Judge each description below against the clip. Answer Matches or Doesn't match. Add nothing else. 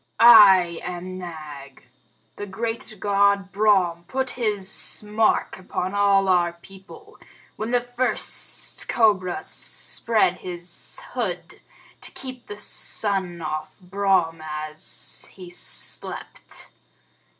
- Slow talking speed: Matches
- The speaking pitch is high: Matches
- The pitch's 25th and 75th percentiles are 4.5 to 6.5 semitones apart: Doesn't match